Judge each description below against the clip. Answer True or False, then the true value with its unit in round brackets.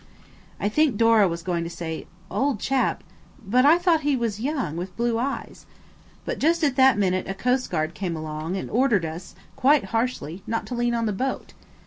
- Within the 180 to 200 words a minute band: True (185 wpm)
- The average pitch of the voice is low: False (230 Hz)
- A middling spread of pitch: False (6.6 semitones)